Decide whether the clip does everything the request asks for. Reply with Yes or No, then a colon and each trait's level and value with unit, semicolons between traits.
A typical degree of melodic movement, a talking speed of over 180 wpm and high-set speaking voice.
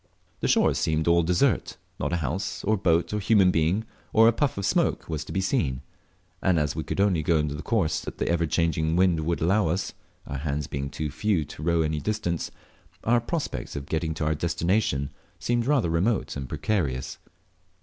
No: average, 4.2 semitones; average, 200 wpm; very low, 85 Hz